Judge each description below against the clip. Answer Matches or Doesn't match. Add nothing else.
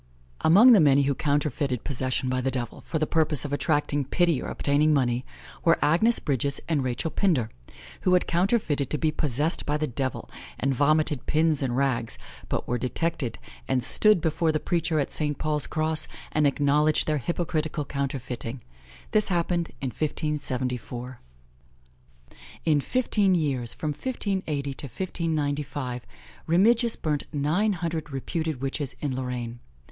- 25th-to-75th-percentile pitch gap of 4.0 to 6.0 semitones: Doesn't match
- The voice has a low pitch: Doesn't match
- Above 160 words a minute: Doesn't match